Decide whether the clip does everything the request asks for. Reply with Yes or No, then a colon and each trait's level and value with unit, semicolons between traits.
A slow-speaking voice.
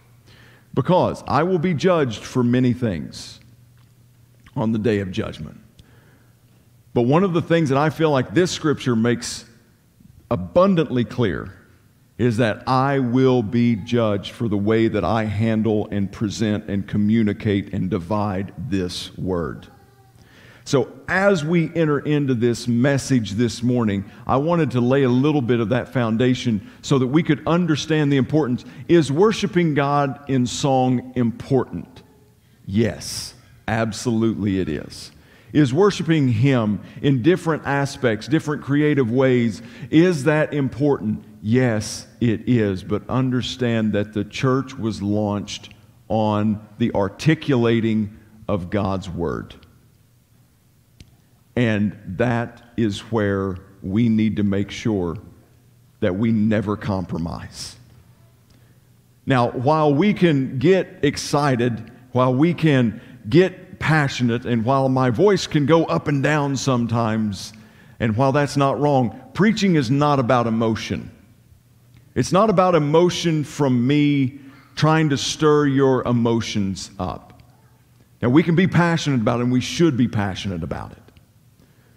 Yes: slow, 130 wpm